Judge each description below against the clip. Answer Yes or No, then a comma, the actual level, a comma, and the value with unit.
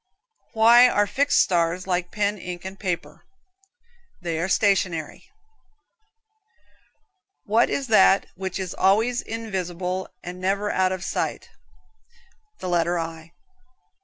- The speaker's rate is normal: No, slow, 120 wpm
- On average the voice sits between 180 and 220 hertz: Yes, high, 190 Hz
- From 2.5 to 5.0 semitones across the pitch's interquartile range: Yes, average, 2.8 semitones